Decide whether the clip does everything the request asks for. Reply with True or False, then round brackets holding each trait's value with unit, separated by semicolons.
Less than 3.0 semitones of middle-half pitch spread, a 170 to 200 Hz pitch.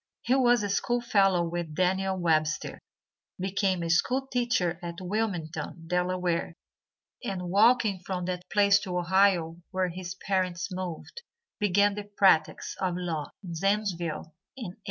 True (2.6 semitones; 185 Hz)